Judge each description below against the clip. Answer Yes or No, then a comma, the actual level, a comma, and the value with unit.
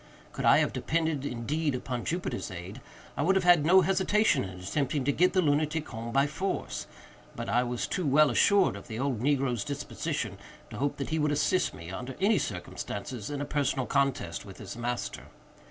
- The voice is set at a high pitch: No, medium, 140 Hz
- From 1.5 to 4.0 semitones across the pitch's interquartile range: No, average, 4.8 semitones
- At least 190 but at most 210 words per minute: Yes, average, 195 wpm